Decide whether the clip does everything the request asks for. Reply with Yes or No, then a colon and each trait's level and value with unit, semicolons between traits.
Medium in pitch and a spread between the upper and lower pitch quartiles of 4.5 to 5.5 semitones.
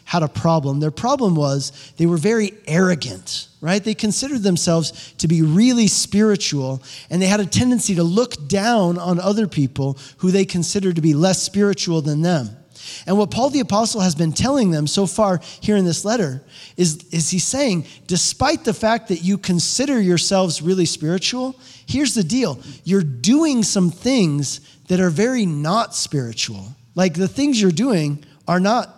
Yes: medium, 180 Hz; average, 5.2 semitones